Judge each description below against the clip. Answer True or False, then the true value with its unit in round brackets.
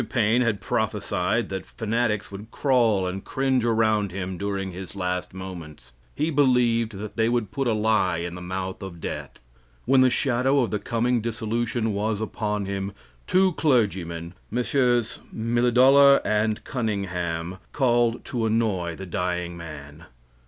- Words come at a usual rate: True (150 wpm)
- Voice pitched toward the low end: True (110 Hz)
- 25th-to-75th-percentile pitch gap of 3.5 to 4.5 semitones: True (4.2 semitones)